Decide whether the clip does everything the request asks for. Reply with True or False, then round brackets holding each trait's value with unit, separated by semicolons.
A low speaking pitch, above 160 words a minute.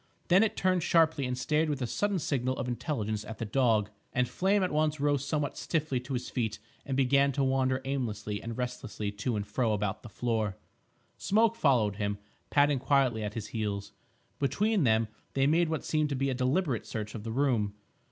True (130 Hz; 200 wpm)